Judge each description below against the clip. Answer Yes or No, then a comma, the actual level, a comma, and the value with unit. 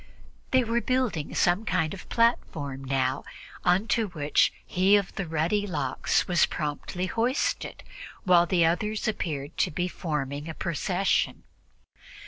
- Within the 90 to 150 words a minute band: Yes, average, 140 wpm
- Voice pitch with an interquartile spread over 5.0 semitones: Yes, wide, 5.4 semitones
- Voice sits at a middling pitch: Yes, medium, 175 Hz